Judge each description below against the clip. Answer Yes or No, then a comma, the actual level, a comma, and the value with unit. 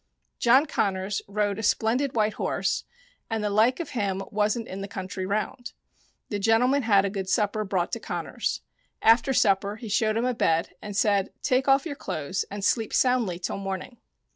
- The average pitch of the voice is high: Yes, high, 210 Hz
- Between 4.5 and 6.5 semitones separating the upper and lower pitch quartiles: No, average, 3.2 semitones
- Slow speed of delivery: No, average, 185 wpm